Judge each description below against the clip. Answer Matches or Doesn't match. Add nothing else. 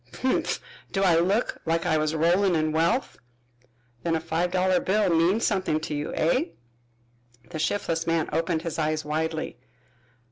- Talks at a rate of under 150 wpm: Doesn't match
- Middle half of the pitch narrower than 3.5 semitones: Matches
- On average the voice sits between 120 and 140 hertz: Doesn't match